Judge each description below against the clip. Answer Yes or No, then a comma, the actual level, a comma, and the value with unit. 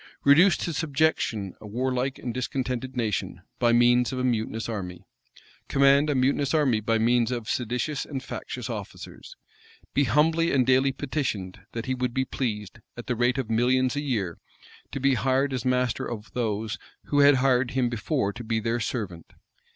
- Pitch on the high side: No, low, 125 Hz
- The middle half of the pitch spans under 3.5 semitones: Yes, average, 3.0 semitones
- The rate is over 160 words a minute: Yes, average, 175 wpm